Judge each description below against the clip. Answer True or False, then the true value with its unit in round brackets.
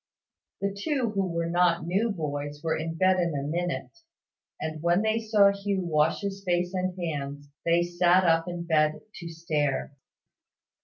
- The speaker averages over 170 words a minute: False (165 wpm)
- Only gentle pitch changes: False (3.1 semitones)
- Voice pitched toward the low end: False (175 Hz)